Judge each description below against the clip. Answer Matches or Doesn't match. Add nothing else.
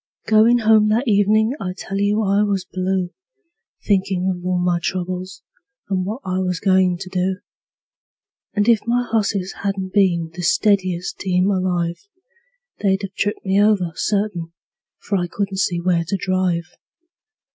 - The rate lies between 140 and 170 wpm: Matches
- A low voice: Doesn't match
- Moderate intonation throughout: Doesn't match